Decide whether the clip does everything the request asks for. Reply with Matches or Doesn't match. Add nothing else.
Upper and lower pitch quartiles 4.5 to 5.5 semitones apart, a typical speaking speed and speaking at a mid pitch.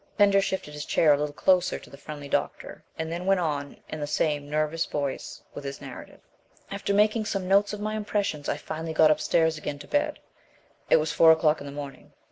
Doesn't match